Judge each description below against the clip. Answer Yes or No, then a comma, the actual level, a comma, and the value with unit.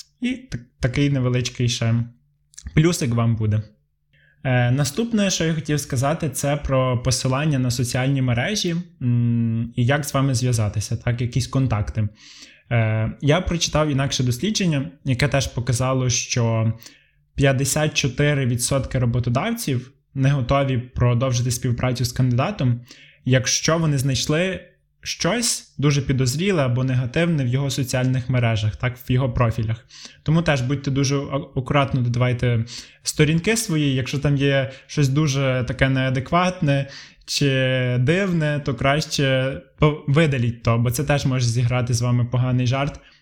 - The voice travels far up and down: No, average, 2.8 semitones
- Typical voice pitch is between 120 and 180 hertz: Yes, low, 135 Hz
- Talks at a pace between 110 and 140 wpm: Yes, average, 130 wpm